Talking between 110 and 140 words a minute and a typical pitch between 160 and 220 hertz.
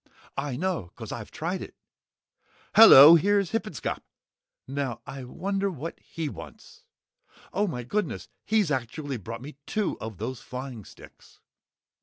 No: slow, 135 wpm; medium, 145 Hz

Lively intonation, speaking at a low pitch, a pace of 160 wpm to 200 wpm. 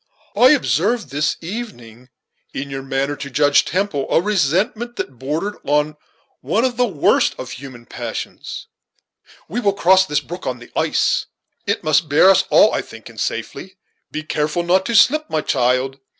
No: wide, 6.5 semitones; medium, 155 Hz; average, 170 wpm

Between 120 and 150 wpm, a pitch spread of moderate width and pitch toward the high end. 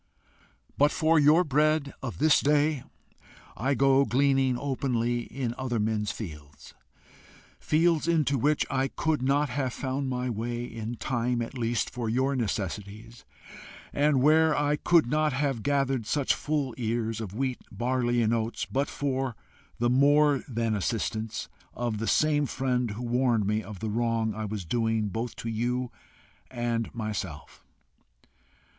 No: average, 145 wpm; average, 3.7 semitones; low, 125 Hz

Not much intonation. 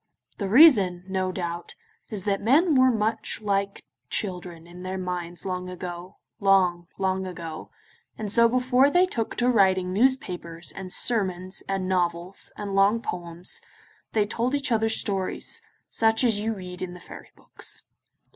No: average, 3.7 semitones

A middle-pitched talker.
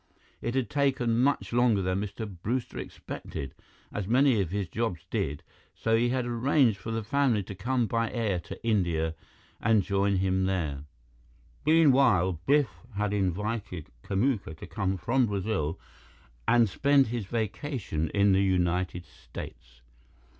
No: low, 105 Hz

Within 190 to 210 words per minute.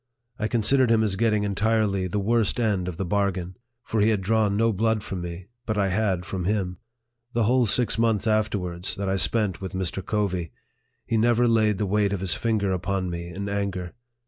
Yes: fast, 205 wpm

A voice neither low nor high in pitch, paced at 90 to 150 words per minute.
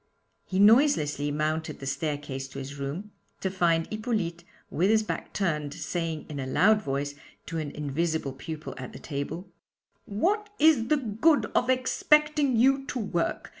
No: medium, 170 Hz; average, 160 wpm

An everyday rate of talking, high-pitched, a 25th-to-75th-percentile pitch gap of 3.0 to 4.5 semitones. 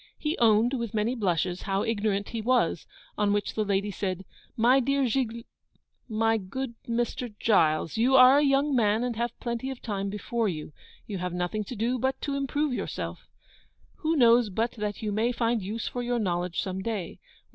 Yes: average, 190 wpm; high, 225 Hz; average, 3.5 semitones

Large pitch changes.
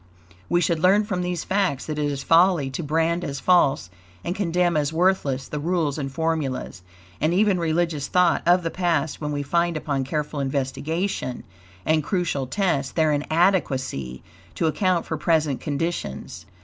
No: average, 3.7 semitones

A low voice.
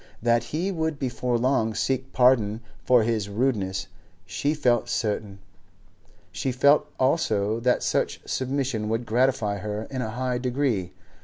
Yes: low, 120 Hz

